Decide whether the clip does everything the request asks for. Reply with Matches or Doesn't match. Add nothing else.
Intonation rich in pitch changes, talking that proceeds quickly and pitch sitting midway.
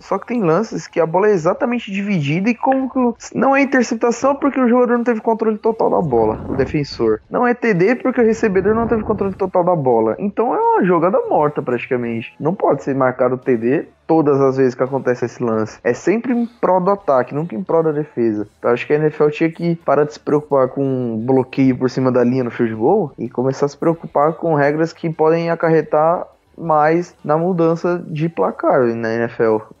Matches